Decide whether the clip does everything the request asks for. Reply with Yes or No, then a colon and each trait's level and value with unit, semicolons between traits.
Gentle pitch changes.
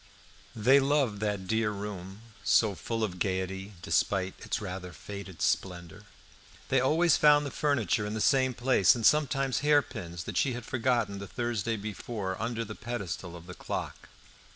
No: average, 4.9 semitones